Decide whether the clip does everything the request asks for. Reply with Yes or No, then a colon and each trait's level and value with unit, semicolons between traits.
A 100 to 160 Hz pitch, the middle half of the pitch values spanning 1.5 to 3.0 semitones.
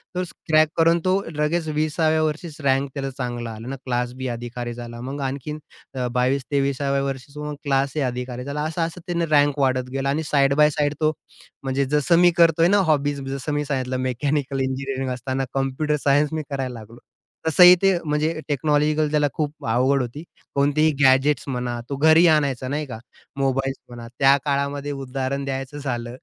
Yes: medium, 140 Hz; narrow, 2.5 semitones